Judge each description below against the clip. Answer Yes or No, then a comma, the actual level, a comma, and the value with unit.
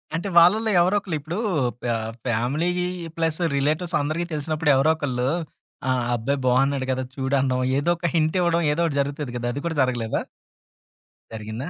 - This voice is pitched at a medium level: Yes, medium, 145 Hz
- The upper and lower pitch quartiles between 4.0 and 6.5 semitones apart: Yes, average, 4.4 semitones